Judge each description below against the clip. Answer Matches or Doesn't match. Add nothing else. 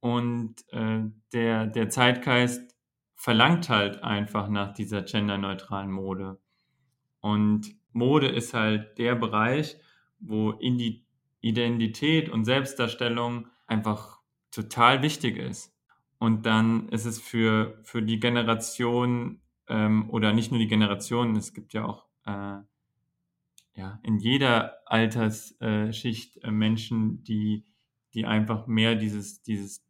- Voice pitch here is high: Doesn't match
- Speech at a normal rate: Doesn't match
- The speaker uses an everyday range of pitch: Doesn't match